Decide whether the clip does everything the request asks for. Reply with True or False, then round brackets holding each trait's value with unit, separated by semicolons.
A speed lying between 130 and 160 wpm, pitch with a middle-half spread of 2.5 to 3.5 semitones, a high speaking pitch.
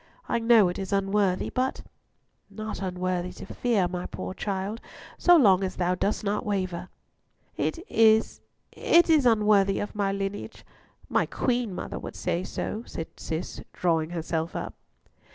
True (155 wpm; 3.2 semitones; 195 Hz)